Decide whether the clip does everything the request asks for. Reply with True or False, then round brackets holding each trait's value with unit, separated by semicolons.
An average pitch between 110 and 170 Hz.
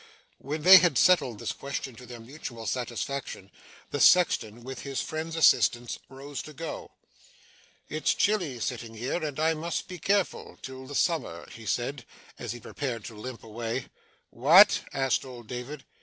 True (135 Hz)